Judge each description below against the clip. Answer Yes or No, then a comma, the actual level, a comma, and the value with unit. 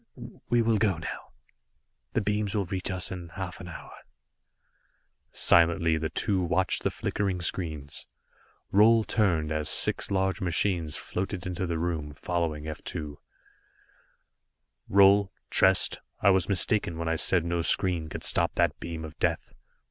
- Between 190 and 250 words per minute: No, average, 150 wpm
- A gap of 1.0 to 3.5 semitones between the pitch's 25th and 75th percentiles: Yes, average, 3.1 semitones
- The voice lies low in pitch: Yes, very low, 90 Hz